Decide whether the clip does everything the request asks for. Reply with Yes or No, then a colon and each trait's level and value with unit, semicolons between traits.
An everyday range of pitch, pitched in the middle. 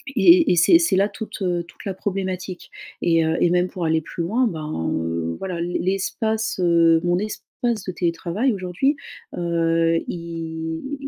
Yes: average, 3.3 semitones; medium, 175 Hz